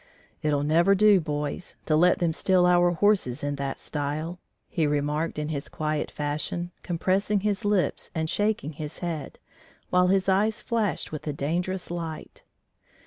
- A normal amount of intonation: Yes, average, 3.8 semitones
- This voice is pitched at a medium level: Yes, medium, 170 Hz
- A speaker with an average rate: Yes, average, 155 wpm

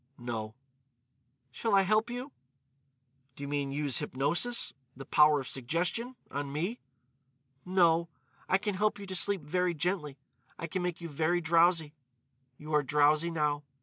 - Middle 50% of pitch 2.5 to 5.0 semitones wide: Yes, average, 4.3 semitones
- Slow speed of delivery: No, average, 145 wpm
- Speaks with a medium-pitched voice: Yes, medium, 165 Hz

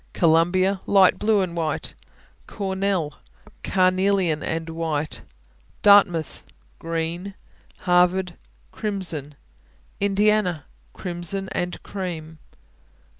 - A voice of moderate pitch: Yes, medium, 180 Hz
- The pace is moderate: No, slow, 75 wpm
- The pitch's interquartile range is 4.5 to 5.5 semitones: No, average, 3.0 semitones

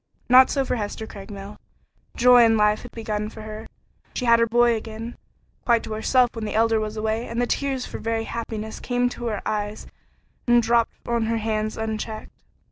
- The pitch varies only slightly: Yes, narrow, 1.7 semitones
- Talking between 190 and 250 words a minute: Yes, average, 195 wpm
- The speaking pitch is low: No, high, 225 Hz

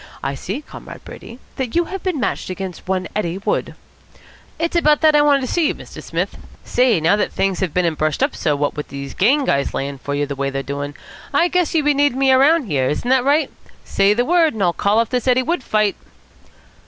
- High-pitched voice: Yes, high, 220 Hz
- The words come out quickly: Yes, fast, 240 wpm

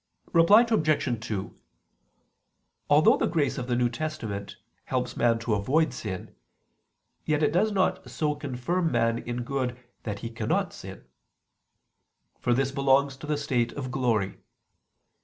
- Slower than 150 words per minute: Yes, average, 140 wpm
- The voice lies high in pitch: No, low, 130 Hz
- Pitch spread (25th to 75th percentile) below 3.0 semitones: No, average, 4.5 semitones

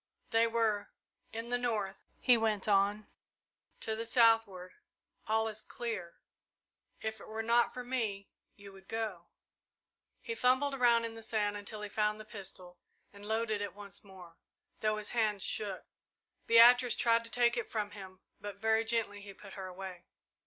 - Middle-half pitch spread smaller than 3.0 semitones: Yes, narrow, 2.5 semitones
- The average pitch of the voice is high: Yes, high, 215 Hz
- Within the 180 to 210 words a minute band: No, average, 165 wpm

